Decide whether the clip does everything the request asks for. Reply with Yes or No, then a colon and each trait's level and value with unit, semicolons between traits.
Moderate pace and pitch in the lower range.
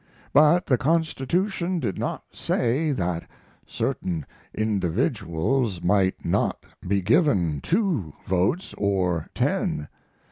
No: slow, 100 wpm; low, 110 Hz